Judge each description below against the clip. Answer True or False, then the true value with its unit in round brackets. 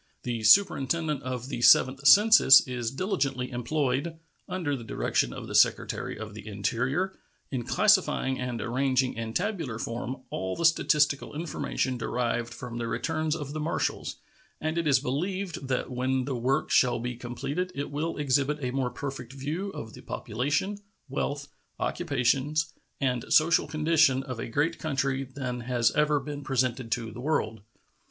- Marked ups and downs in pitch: False (3.7 semitones)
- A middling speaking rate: True (160 wpm)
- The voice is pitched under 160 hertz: True (135 Hz)